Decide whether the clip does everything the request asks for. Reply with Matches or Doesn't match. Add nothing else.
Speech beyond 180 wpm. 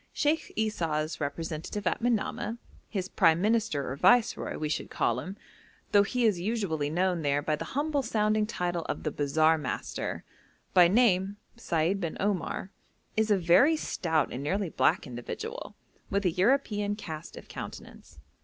Doesn't match